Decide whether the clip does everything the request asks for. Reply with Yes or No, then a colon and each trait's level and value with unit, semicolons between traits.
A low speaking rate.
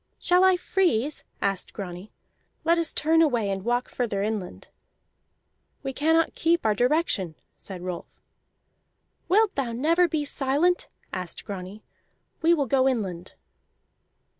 Yes: slow, 130 wpm